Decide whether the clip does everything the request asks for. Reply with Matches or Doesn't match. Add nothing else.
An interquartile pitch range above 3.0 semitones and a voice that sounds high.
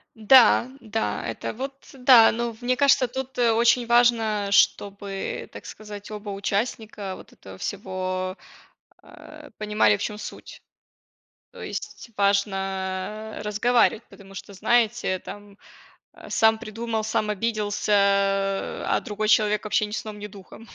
Doesn't match